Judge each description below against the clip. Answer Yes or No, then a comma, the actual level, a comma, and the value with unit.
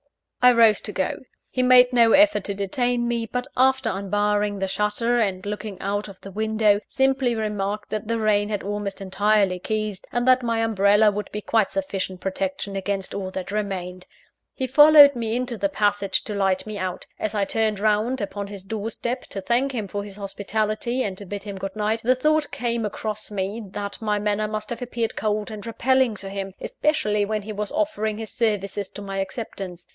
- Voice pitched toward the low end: No, high, 210 Hz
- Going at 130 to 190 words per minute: No, average, 200 wpm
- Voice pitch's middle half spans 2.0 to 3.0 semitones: Yes, narrow, 2.6 semitones